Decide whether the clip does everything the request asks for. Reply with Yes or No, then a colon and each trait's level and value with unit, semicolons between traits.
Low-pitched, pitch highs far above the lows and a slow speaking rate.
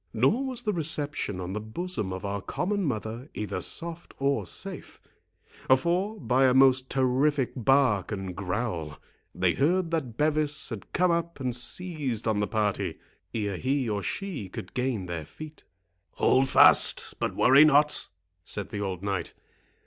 No: low, 130 Hz; wide, 7.0 semitones; average, 155 wpm